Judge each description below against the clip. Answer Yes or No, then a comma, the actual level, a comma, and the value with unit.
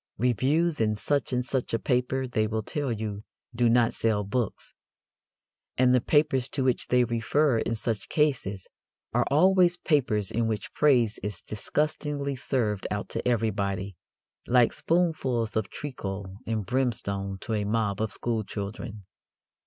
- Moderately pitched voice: No, low, 115 Hz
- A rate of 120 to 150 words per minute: Yes, average, 145 wpm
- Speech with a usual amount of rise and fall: Yes, average, 4.1 semitones